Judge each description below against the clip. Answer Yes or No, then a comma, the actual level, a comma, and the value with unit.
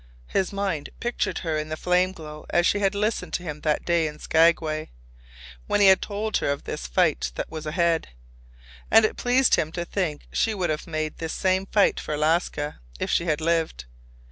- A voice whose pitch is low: No, medium, 170 Hz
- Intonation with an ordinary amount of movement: Yes, average, 3.9 semitones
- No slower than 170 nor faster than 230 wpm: Yes, average, 200 wpm